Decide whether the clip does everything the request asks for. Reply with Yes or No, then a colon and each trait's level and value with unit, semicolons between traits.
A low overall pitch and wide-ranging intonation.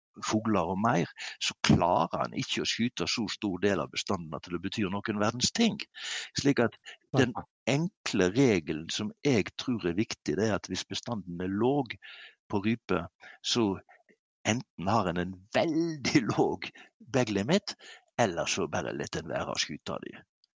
Yes: low, 110 Hz; wide, 6.3 semitones